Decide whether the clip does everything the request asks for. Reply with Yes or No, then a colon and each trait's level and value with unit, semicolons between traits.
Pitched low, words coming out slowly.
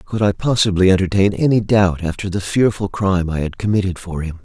No: very low, 95 Hz; fast, 205 wpm